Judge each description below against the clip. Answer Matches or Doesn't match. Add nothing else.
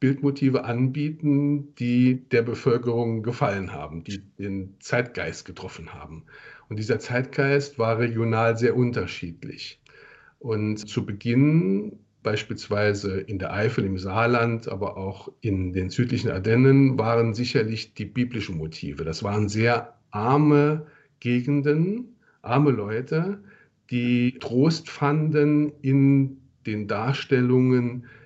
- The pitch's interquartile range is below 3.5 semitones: Doesn't match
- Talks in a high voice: Doesn't match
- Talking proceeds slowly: Matches